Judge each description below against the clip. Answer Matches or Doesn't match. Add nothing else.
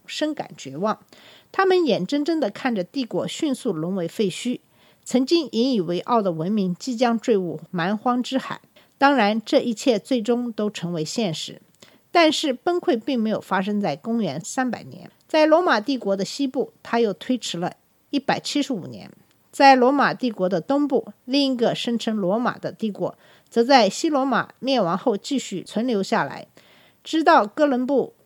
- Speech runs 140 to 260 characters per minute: Matches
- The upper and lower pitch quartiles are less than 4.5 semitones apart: Doesn't match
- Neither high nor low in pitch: Doesn't match